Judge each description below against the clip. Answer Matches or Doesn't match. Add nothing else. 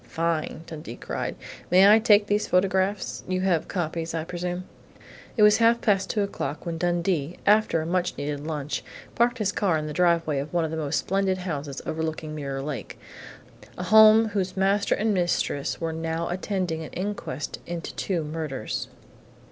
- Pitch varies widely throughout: Doesn't match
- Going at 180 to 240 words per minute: Doesn't match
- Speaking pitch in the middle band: Matches